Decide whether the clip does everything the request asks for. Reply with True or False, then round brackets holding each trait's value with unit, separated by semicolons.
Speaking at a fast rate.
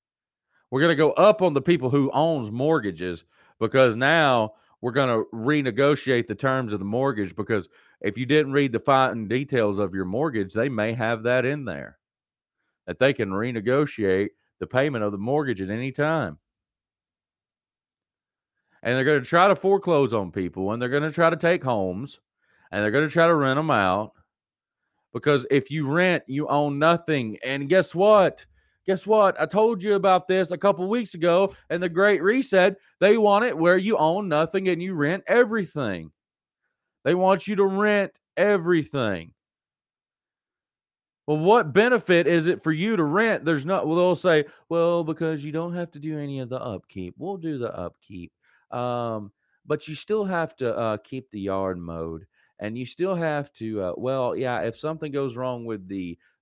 False (185 wpm)